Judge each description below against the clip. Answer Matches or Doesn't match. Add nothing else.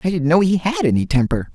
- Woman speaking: Doesn't match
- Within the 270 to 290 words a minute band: Matches